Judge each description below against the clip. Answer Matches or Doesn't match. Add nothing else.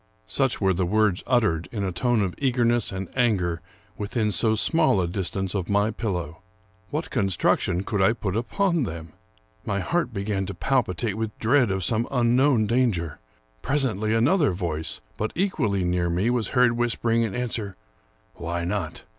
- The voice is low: Matches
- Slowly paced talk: Doesn't match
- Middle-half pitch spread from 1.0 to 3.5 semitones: Doesn't match